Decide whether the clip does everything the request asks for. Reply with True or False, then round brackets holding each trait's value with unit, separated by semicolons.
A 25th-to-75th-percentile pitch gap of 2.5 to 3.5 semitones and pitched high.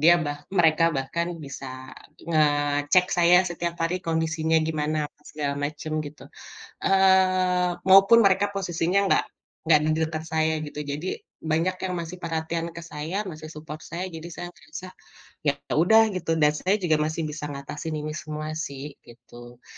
False (2.8 semitones; 160 Hz)